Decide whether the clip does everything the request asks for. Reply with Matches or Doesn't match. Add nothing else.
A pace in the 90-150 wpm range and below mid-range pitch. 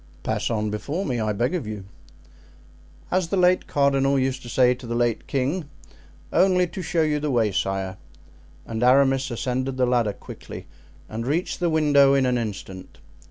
Doesn't match